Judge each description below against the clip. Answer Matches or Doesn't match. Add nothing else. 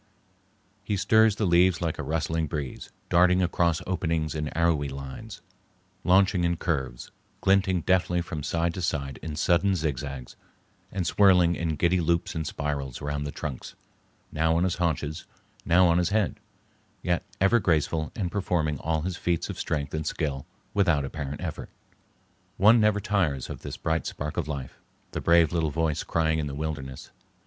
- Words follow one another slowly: Doesn't match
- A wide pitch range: Doesn't match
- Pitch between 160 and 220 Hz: Doesn't match